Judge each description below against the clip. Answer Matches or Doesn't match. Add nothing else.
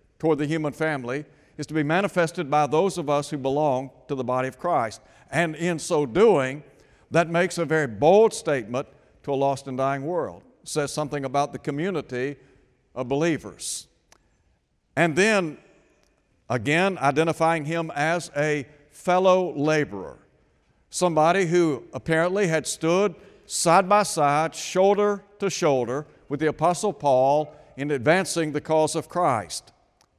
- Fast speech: Doesn't match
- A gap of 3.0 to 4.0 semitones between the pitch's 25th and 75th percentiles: Matches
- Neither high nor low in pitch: Matches